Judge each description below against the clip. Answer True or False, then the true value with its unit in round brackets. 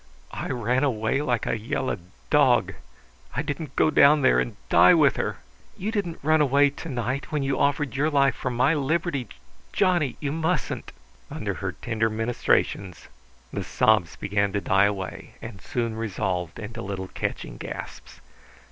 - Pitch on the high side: False (125 Hz)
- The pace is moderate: True (160 wpm)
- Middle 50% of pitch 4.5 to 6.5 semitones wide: True (5.5 semitones)